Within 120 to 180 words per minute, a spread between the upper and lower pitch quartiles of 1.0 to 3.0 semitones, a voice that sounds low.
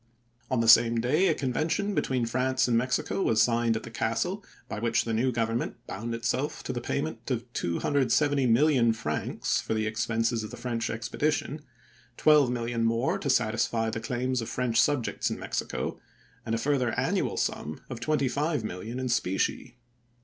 Yes: average, 165 wpm; average, 2.7 semitones; low, 120 Hz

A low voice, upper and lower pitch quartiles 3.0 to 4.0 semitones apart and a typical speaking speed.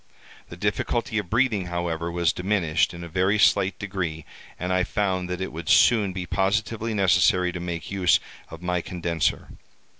No: very low, 90 Hz; narrow, 2.4 semitones; average, 170 wpm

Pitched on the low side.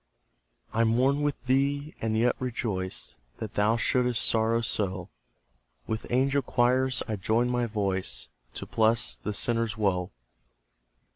Yes: low, 115 Hz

